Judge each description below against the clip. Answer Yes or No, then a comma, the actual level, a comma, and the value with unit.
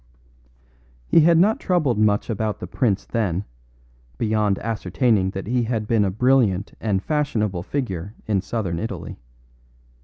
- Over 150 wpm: No, average, 140 wpm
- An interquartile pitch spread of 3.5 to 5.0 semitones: Yes, average, 4.1 semitones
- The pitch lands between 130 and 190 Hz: No, low, 110 Hz